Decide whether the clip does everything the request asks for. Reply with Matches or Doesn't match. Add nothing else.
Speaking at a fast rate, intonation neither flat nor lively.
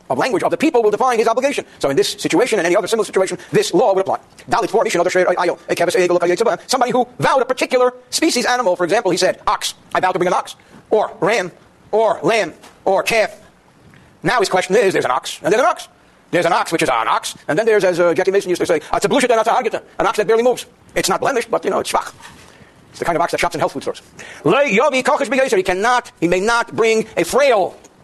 Doesn't match